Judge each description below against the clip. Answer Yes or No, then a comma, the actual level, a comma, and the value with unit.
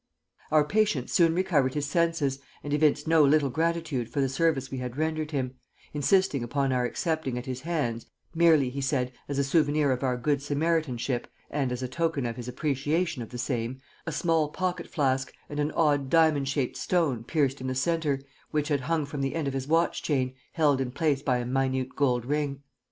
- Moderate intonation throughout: Yes, average, 3.4 semitones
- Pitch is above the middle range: No, medium, 140 Hz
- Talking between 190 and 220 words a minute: Yes, average, 200 wpm